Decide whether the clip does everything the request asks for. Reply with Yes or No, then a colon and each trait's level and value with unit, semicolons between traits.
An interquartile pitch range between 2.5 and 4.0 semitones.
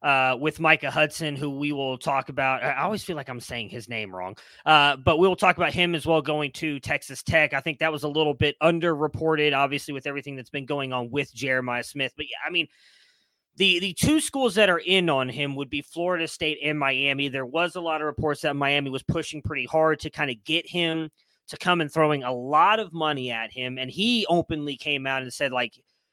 Yes: average, 3.0 semitones